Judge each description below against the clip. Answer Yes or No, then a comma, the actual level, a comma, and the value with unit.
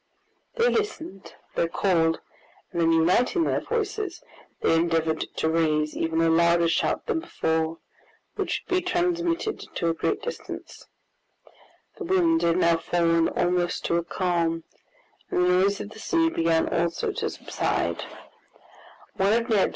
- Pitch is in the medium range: Yes, medium, 175 Hz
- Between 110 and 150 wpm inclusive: Yes, average, 140 wpm